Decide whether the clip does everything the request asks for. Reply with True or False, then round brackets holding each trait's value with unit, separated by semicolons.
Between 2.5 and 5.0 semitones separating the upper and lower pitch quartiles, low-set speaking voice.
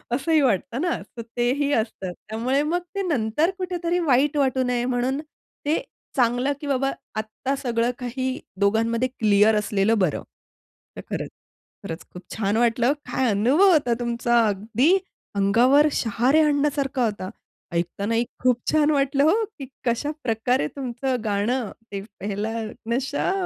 False (4.2 semitones; 245 Hz)